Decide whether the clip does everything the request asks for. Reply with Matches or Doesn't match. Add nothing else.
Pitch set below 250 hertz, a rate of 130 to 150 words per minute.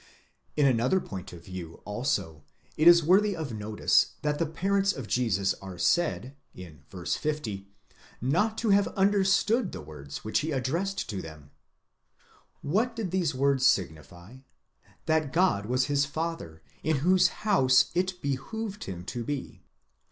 Matches